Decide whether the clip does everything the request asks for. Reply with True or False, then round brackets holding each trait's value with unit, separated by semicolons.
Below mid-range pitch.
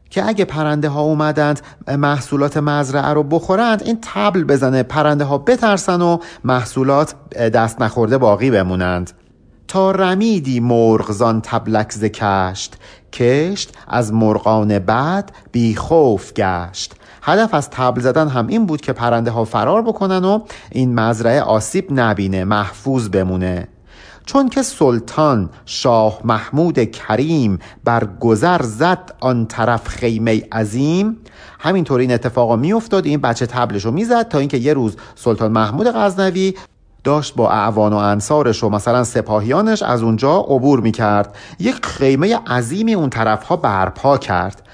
True (125 Hz)